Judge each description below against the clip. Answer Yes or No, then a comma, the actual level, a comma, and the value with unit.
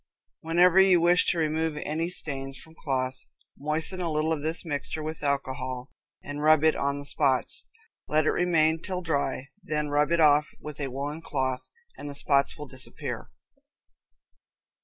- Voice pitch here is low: No, medium, 150 Hz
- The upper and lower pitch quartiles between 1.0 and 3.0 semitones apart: Yes, narrow, 2.4 semitones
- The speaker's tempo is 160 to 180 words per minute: Yes, average, 165 wpm